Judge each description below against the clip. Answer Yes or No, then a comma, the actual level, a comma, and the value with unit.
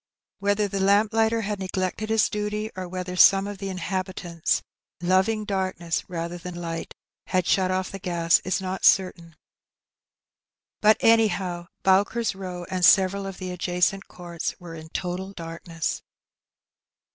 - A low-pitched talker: No, medium, 185 Hz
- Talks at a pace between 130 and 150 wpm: Yes, average, 145 wpm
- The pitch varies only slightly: Yes, narrow, 2.2 semitones